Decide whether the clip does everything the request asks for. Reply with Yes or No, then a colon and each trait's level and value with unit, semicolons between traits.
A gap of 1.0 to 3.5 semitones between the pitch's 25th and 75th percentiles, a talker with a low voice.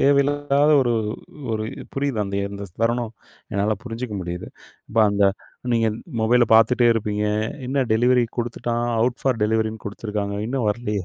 Yes: average, 2.9 semitones; low, 115 Hz